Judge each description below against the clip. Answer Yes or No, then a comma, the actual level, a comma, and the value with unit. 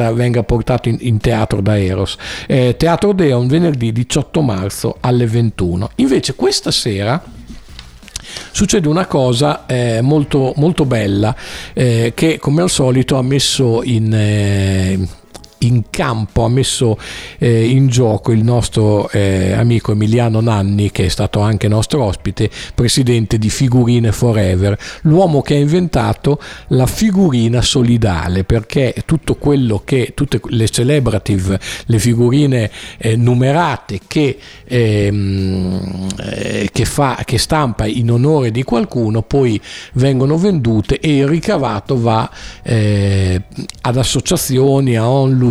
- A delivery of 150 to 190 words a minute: No, average, 130 wpm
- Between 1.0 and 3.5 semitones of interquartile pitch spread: No, average, 4.3 semitones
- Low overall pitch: Yes, low, 120 Hz